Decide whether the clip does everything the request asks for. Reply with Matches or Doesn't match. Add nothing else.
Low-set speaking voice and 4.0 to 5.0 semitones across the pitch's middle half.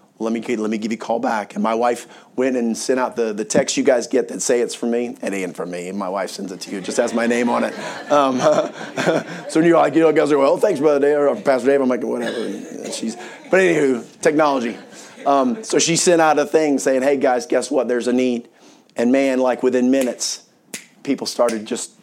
Doesn't match